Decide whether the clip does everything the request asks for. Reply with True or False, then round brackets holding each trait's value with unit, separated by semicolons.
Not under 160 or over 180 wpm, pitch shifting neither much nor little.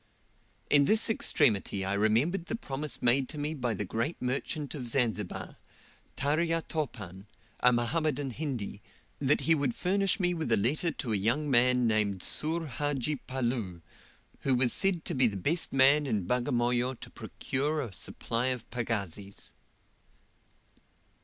False (150 wpm; 4.9 semitones)